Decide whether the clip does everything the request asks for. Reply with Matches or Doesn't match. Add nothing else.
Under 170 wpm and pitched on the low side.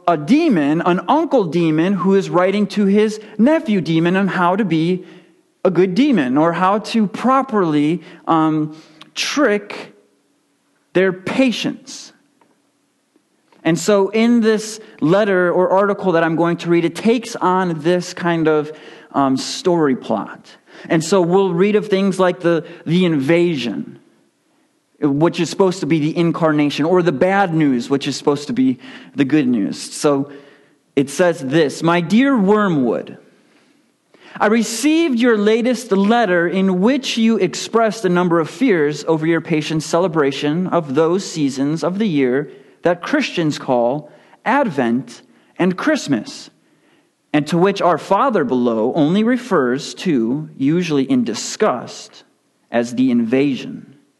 Doesn't match